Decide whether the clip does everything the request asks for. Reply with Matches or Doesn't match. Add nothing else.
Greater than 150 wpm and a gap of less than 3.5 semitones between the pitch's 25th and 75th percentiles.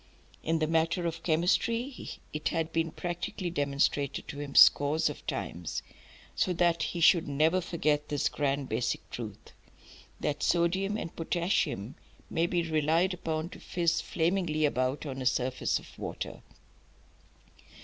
Doesn't match